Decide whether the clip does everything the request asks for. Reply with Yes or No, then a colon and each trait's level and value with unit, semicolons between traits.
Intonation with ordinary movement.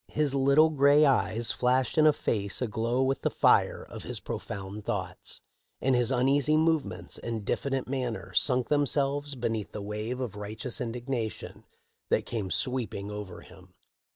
Yes: average, 4.0 semitones